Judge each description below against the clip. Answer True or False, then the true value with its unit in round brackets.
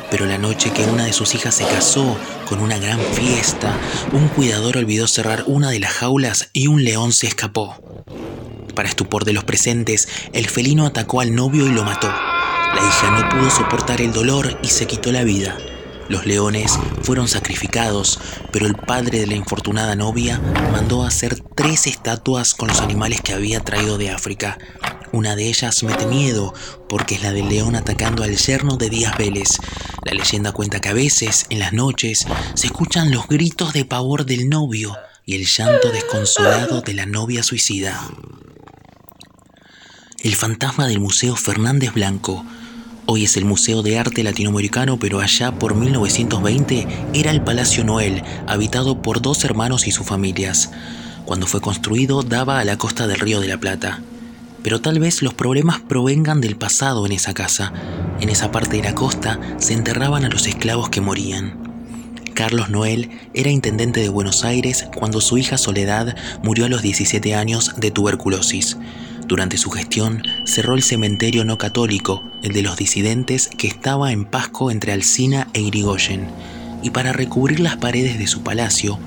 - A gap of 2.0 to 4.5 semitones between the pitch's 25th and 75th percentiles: True (3.8 semitones)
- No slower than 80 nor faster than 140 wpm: False (170 wpm)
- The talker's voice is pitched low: True (115 Hz)